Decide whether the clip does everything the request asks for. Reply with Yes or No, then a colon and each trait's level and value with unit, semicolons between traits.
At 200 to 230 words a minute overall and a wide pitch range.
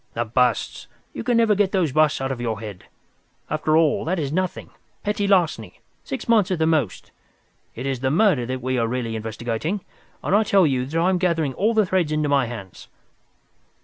Yes: fast, 205 wpm; wide, 7.0 semitones